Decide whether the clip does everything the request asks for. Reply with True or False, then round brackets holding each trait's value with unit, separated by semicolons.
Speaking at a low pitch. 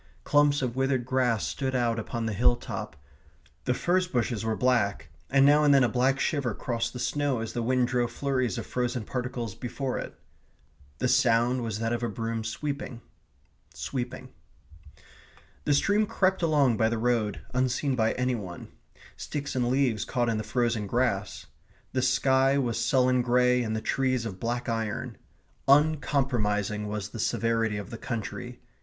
True (125 Hz)